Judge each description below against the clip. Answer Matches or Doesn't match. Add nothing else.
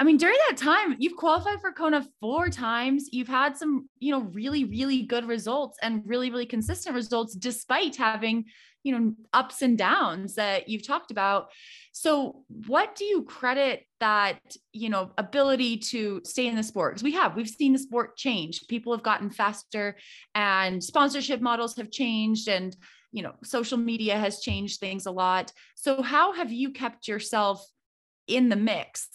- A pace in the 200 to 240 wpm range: Doesn't match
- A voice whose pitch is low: Doesn't match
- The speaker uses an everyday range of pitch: Matches